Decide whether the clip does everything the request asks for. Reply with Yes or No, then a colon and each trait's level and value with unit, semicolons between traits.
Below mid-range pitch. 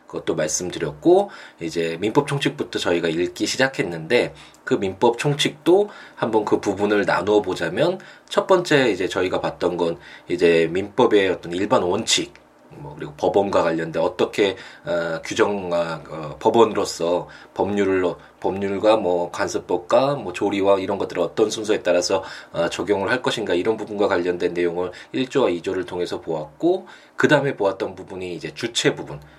Yes: very low, 95 Hz